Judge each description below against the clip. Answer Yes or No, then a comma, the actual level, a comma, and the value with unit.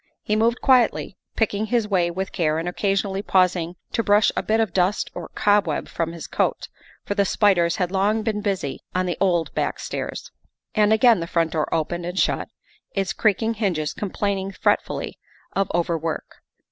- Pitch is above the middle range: Yes, high, 195 Hz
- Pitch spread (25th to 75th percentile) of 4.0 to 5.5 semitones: No, average, 3.4 semitones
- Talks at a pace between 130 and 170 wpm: No, average, 180 wpm